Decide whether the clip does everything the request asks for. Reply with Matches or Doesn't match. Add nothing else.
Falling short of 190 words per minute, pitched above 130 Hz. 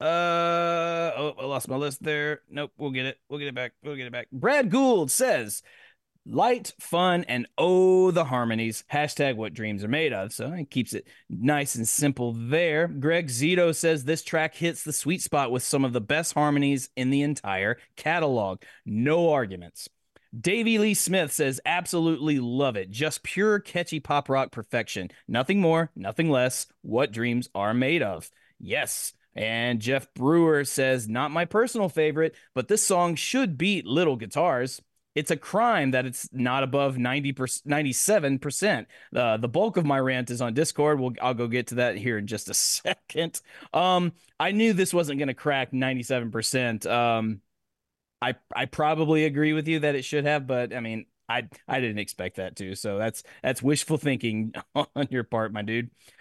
Matches